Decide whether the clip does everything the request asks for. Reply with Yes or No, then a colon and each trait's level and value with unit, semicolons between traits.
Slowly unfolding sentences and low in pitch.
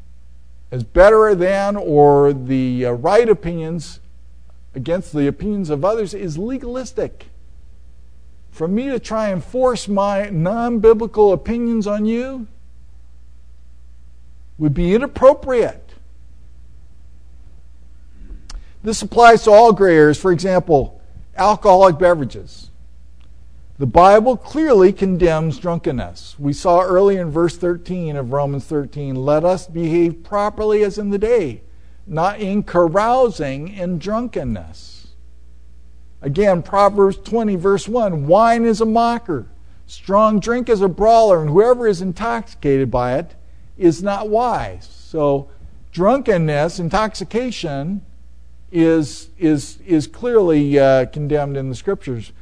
No: slow, 115 wpm; medium, 165 Hz